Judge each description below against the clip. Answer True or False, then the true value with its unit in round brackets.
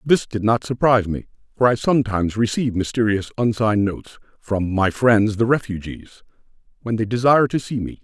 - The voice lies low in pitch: True (110 Hz)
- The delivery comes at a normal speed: True (170 wpm)